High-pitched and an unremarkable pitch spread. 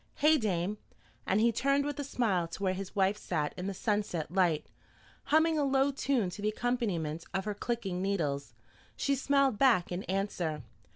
No: high, 205 Hz; wide, 6.8 semitones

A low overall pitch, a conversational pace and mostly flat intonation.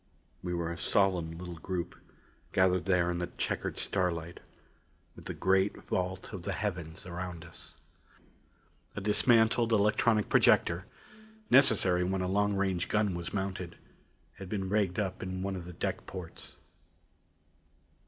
Yes: very low, 95 Hz; average, 145 wpm; narrow, 2.3 semitones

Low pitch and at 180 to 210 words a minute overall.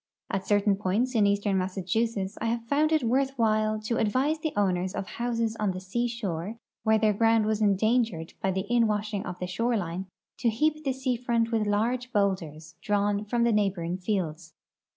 No: high, 215 Hz; average, 185 wpm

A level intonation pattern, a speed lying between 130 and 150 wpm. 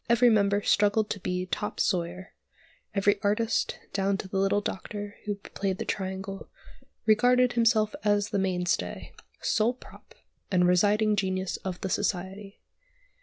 Yes: narrow, 1.9 semitones; average, 140 wpm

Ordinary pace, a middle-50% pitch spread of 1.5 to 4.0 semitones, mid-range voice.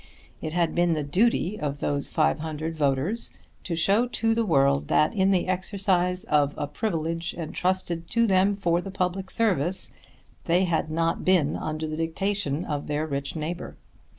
Yes: average, 165 wpm; average, 3.6 semitones; medium, 170 Hz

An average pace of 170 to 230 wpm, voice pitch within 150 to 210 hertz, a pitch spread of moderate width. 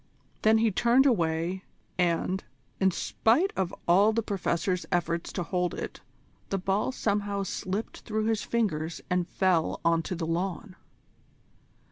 No: average, 140 wpm; high, 190 Hz; average, 3.9 semitones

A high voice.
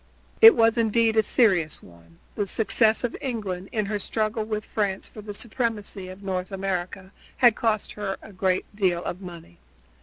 Yes: high, 205 Hz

